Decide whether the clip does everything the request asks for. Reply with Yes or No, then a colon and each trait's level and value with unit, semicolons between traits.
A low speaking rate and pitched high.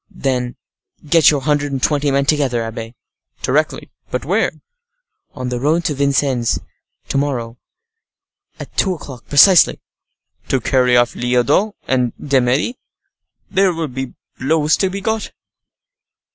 No: slow, 130 wpm; medium, 140 Hz